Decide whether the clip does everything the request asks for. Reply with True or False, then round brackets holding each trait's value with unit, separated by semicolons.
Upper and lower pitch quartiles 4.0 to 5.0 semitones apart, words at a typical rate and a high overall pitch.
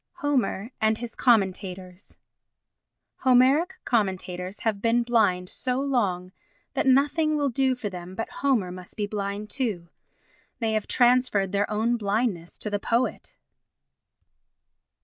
False (4.7 semitones; 130 wpm; 220 Hz)